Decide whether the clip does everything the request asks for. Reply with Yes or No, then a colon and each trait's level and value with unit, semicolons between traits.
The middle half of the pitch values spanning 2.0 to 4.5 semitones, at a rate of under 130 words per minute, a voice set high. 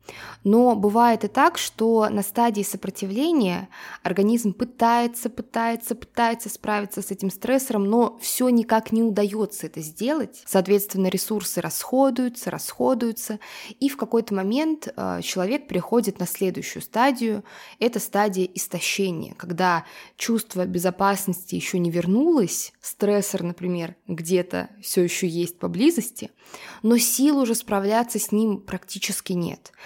Yes: average, 3.8 semitones; average, 120 wpm; high, 210 Hz